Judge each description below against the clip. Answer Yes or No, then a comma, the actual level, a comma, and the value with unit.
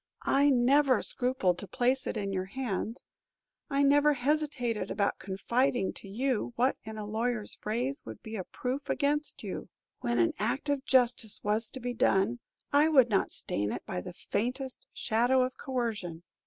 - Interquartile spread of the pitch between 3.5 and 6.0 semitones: Yes, average, 4.2 semitones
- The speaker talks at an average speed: Yes, average, 170 wpm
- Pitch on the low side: No, high, 245 Hz